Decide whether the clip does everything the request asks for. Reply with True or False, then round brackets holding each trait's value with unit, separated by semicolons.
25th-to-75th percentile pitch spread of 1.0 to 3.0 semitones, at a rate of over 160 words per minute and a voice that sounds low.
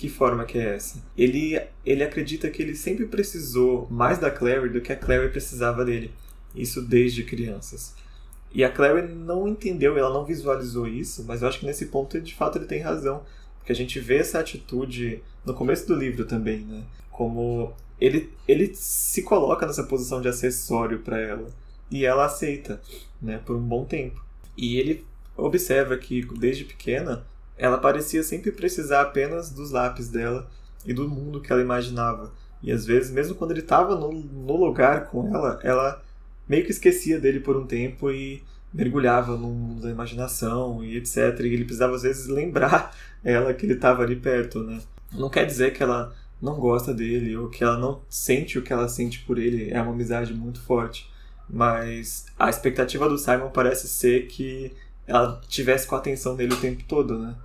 True (2.6 semitones; 185 wpm; 125 Hz)